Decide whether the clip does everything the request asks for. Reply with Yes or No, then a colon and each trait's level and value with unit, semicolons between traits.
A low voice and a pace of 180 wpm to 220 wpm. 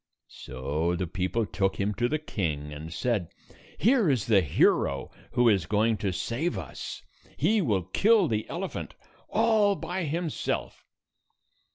No: low, 110 Hz; average, 150 wpm